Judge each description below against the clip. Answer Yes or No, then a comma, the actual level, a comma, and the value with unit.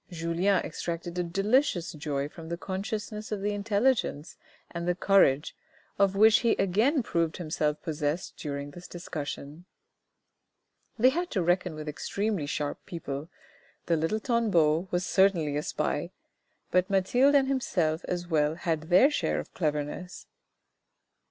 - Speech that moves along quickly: No, average, 140 wpm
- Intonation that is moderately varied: Yes, average, 4.5 semitones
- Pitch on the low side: No, medium, 175 Hz